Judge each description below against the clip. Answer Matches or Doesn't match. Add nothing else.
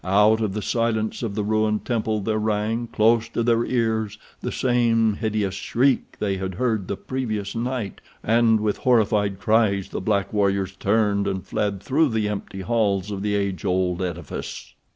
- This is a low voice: Matches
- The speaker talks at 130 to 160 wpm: Doesn't match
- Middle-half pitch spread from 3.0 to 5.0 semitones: Doesn't match